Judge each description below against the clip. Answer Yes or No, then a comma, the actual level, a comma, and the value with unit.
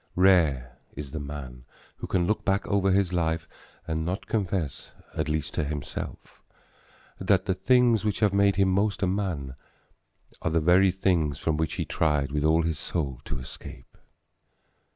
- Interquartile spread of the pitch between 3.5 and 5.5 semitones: Yes, average, 4.5 semitones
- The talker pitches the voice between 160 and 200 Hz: No, very low, 85 Hz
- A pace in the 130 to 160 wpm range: No, average, 170 wpm